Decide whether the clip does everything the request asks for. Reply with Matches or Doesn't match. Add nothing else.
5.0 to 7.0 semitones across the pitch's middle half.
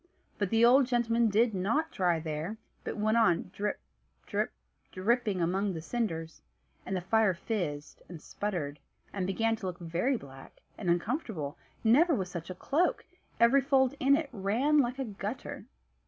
Matches